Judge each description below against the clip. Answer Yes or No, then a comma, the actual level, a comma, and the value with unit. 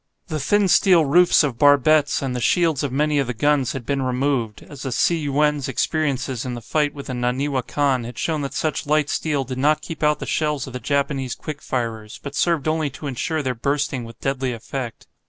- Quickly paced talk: Yes, fast, 220 wpm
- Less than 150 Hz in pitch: Yes, medium, 140 Hz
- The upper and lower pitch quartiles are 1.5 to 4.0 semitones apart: Yes, average, 2.8 semitones